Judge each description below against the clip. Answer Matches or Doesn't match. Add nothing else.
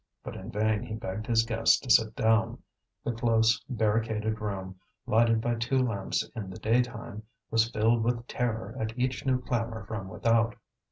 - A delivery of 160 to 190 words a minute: Matches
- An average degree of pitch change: Doesn't match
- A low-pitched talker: Matches